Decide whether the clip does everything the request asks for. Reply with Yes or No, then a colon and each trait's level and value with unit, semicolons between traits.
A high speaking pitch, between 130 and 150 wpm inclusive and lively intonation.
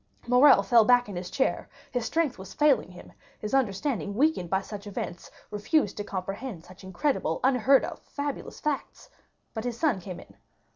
No: high, 225 Hz; average, 175 wpm; wide, 5.8 semitones